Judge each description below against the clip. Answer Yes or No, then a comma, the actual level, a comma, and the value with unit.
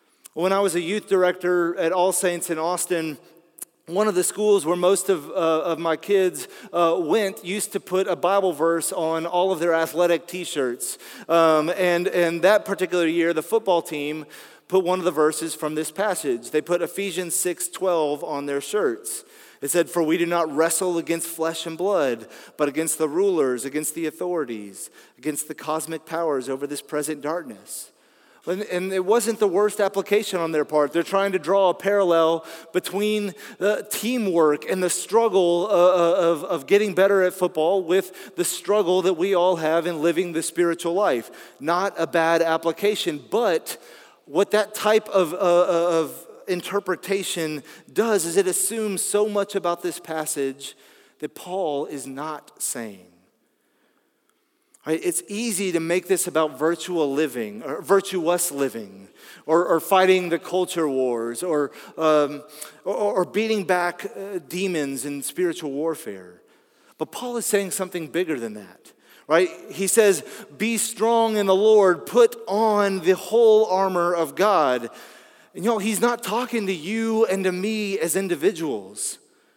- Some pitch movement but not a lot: Yes, average, 3.5 semitones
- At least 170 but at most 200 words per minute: No, average, 160 wpm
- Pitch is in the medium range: Yes, medium, 180 Hz